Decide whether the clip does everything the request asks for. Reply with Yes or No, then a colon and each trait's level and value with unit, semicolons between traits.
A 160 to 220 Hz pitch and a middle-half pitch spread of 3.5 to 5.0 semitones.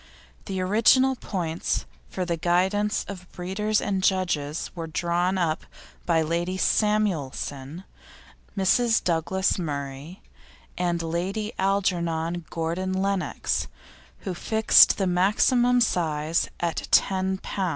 No: medium, 185 Hz; average, 2.9 semitones